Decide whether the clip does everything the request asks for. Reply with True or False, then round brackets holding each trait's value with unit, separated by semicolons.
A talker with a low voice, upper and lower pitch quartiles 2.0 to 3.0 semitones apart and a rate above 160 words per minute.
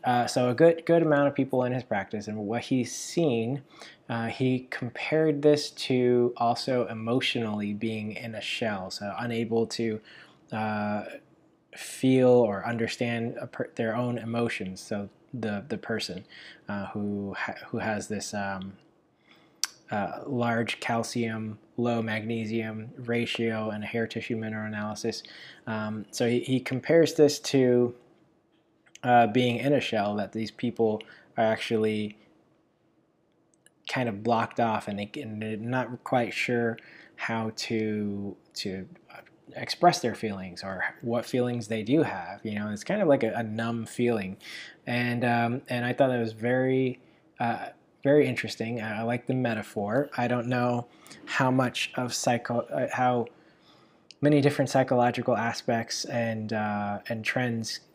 False (120 Hz; 2.5 semitones; 145 wpm)